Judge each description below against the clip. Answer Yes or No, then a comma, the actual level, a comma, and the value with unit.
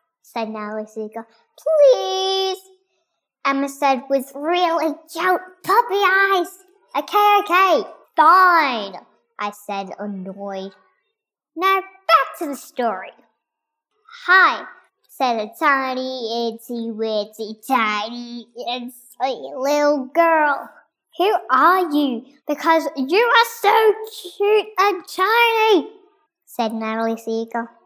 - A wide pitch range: Yes, wide, 8.0 semitones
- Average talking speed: No, slow, 95 wpm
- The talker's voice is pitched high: Yes, very high, 305 Hz